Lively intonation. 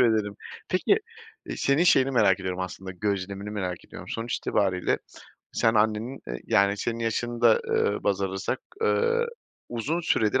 No: average, 3.9 semitones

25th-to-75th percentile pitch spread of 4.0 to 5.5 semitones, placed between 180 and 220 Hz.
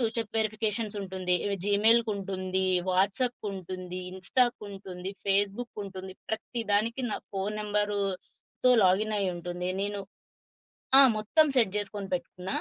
No: narrow, 2.4 semitones; high, 200 Hz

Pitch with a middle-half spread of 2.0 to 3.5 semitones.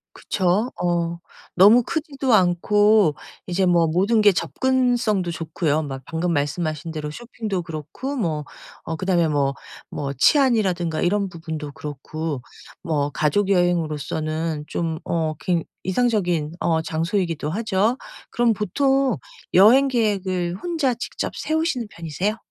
No: wide, 5.4 semitones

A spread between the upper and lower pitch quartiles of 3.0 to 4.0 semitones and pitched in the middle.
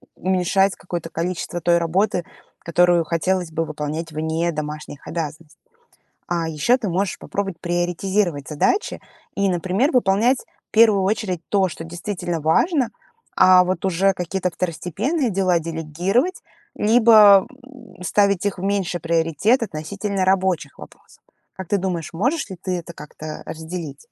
Yes: average, 3.3 semitones; medium, 180 Hz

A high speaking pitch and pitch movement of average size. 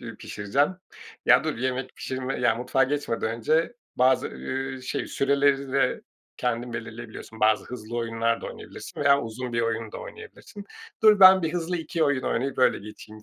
No: low, 130 Hz; average, 3.7 semitones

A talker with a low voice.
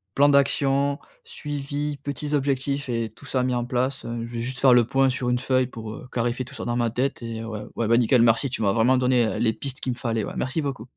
Yes: low, 125 Hz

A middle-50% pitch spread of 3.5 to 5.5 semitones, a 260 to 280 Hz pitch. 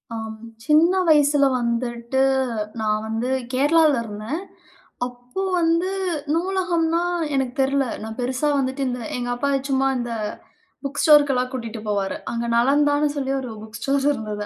Yes: average, 3.8 semitones; very high, 265 Hz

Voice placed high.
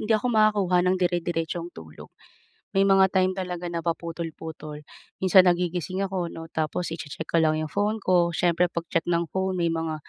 No: medium, 175 Hz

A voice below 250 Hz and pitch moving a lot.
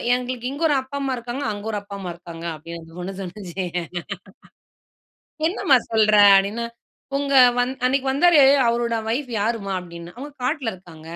Yes: high, 230 Hz; wide, 6.0 semitones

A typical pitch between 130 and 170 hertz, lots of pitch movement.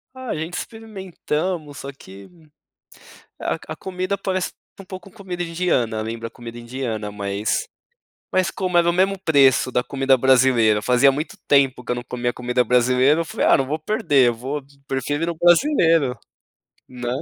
Yes: medium, 140 Hz; wide, 6.3 semitones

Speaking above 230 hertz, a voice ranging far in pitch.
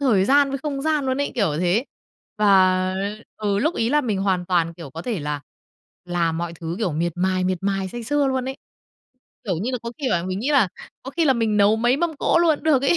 No: high, 210 Hz; wide, 6.8 semitones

